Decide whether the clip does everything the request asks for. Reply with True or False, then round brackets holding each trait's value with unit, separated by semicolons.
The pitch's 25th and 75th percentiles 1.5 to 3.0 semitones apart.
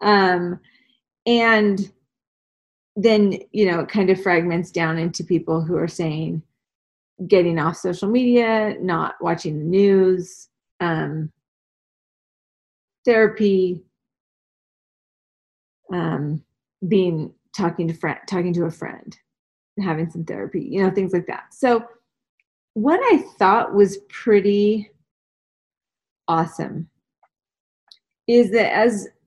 False (4.0 semitones)